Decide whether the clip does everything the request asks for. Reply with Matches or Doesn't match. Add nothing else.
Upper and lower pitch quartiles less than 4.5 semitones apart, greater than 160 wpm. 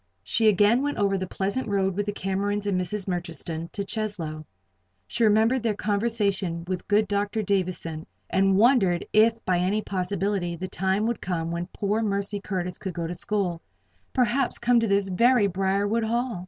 Matches